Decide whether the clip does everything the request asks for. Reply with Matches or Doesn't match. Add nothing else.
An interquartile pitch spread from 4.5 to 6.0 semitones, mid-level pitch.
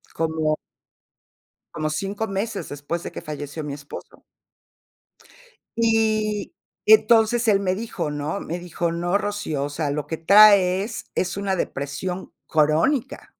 Matches